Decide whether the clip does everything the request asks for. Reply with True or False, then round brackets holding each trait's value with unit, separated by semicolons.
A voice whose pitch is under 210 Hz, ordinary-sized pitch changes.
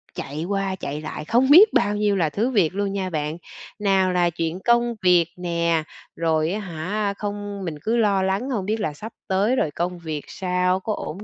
True (190 Hz; 3.6 semitones)